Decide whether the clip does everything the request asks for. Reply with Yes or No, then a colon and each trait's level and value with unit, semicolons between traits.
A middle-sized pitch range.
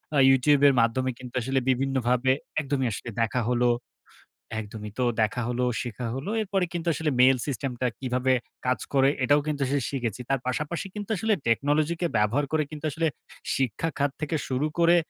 Yes: average, 3.2 semitones